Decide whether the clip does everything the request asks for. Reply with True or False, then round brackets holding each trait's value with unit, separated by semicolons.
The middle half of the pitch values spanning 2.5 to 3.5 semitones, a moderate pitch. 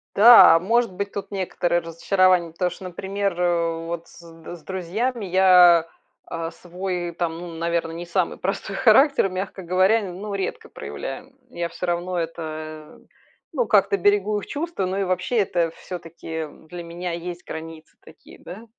True (2.8 semitones; 180 Hz)